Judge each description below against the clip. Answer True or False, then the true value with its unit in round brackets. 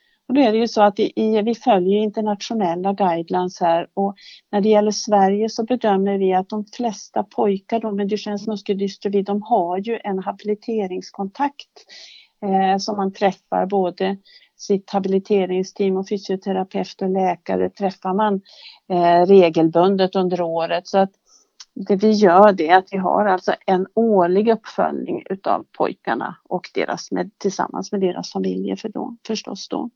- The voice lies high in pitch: True (200 Hz)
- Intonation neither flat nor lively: False (2.1 semitones)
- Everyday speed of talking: True (155 wpm)